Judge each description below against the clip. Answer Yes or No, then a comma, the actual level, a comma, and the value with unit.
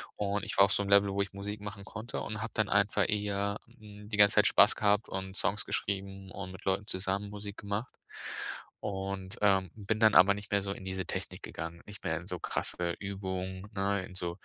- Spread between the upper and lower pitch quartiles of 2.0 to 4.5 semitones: No, narrow, 1.3 semitones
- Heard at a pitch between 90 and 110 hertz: Yes, low, 100 Hz